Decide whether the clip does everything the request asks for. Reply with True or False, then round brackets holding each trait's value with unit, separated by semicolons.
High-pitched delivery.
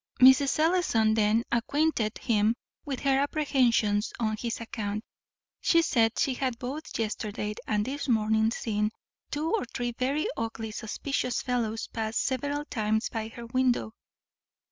True (235 Hz)